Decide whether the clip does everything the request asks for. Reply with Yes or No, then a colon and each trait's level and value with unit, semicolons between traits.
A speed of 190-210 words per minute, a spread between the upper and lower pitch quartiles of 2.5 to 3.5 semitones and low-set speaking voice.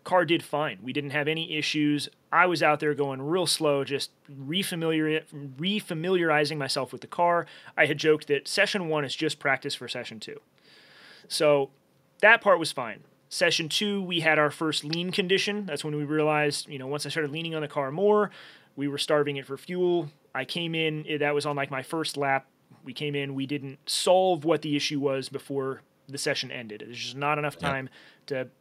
No: fast, 205 wpm; average, 2.9 semitones; medium, 150 Hz